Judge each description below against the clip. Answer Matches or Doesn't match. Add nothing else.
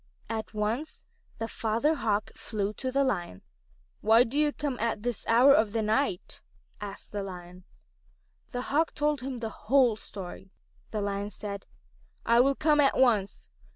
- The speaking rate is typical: Matches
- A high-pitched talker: Matches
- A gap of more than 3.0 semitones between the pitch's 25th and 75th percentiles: Matches